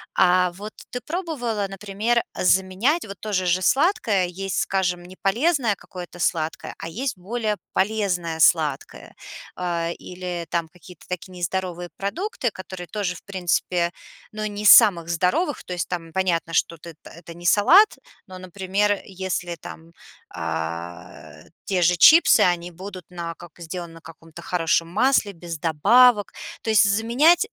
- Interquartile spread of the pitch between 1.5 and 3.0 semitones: No, average, 3.5 semitones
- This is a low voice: No, medium, 185 Hz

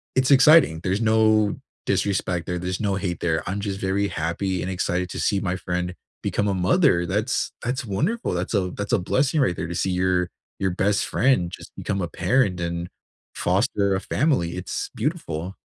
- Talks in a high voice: No, very low, 95 Hz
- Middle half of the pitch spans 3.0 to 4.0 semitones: Yes, average, 3.5 semitones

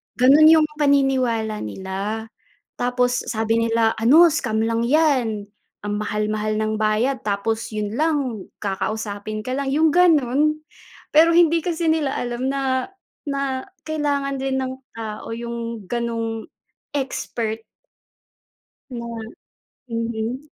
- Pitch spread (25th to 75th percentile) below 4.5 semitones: Yes, average, 4.1 semitones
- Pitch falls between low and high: No, high, 235 Hz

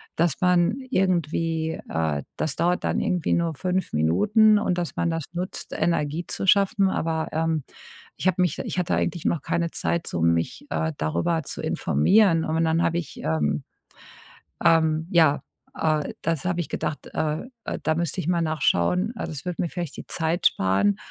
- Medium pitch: Yes, medium, 165 Hz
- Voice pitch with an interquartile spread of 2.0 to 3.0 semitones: Yes, narrow, 2.6 semitones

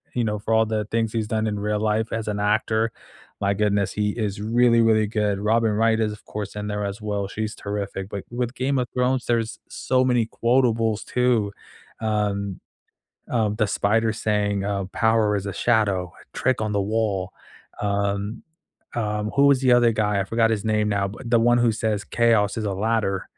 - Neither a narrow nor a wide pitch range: No, narrow, 1.9 semitones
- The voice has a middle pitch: No, low, 110 Hz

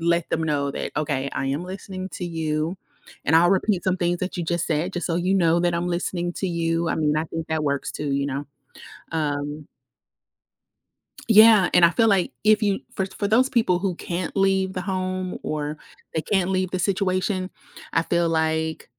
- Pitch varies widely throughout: No, average, 2.8 semitones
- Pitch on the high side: No, medium, 175 Hz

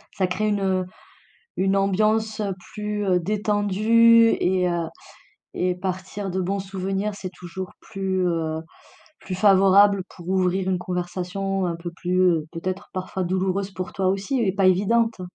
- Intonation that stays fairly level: Yes, narrow, 1.8 semitones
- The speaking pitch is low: No, high, 190 Hz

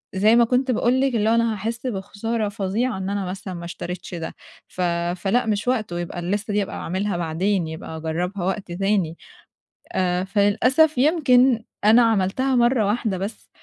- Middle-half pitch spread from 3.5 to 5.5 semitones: Yes, average, 4.1 semitones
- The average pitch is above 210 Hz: No, high, 205 Hz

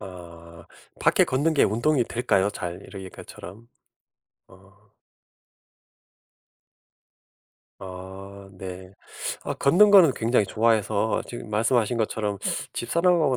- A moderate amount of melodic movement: Yes, average, 4.6 semitones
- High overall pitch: No, low, 105 Hz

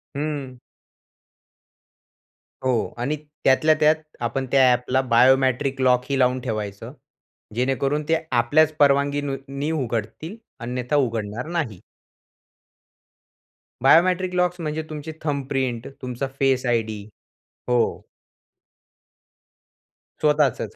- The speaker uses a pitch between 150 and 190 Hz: No, low, 135 Hz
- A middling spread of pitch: Yes, average, 3.1 semitones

